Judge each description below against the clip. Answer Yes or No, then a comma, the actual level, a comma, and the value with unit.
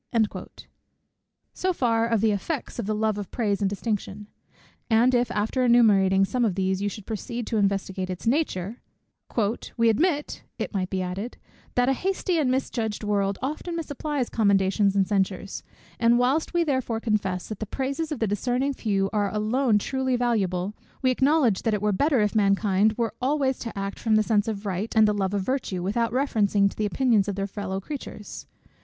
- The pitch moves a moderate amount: Yes, average, 4.1 semitones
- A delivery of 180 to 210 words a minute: Yes, average, 185 wpm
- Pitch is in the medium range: No, high, 215 Hz